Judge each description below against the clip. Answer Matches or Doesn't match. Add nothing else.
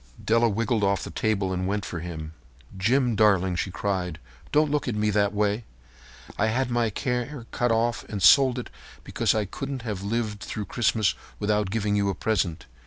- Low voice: Matches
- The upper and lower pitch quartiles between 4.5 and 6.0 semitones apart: Doesn't match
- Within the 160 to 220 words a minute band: Matches